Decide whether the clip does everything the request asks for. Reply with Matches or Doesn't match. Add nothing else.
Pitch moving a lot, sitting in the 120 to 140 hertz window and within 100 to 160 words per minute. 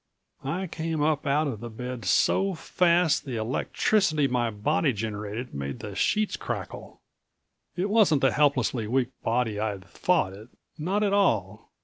Matches